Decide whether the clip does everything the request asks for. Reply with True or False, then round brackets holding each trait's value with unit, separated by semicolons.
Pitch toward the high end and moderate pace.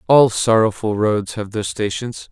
False (110 Hz; 155 wpm)